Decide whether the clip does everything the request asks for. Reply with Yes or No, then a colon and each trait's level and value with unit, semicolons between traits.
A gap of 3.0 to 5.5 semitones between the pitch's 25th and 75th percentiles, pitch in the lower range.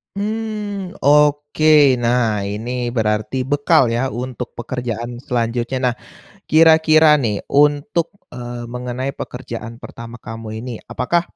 Yes: average, 4.8 semitones; low, 125 Hz